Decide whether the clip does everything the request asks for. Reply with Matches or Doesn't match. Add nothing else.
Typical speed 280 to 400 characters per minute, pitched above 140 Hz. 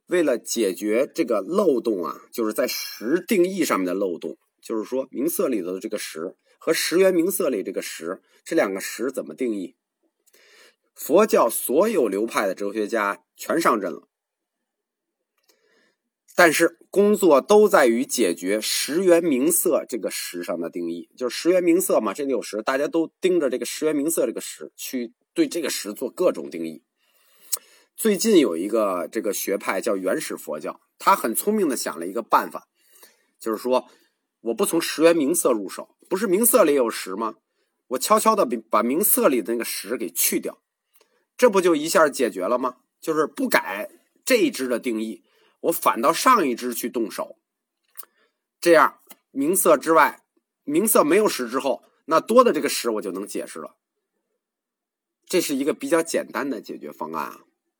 Doesn't match